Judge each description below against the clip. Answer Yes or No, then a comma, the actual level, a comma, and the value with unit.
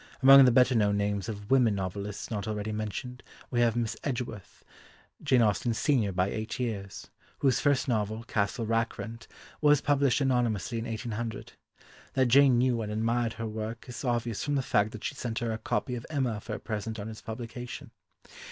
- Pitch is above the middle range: No, low, 115 Hz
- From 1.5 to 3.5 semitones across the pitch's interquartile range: Yes, narrow, 2.6 semitones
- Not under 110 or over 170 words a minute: No, average, 185 wpm